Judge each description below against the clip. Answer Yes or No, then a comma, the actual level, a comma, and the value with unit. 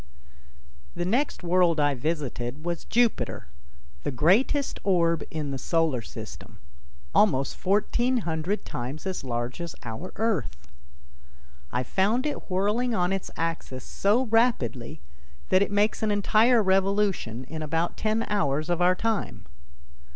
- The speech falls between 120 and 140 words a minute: Yes, slow, 135 wpm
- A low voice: No, medium, 175 Hz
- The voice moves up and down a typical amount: No, wide, 6.4 semitones